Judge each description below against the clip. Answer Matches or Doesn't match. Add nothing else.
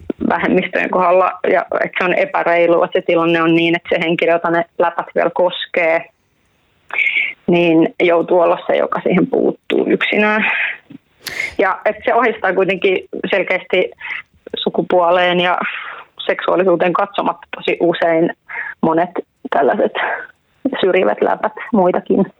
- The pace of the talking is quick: Doesn't match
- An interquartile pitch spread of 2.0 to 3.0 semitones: Matches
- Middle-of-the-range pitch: Matches